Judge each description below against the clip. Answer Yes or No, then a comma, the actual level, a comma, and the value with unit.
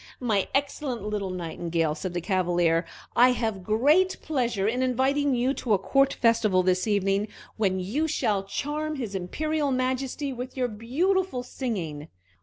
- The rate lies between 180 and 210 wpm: No, average, 150 wpm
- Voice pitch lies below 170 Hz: No, high, 230 Hz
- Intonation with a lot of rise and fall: Yes, wide, 6.0 semitones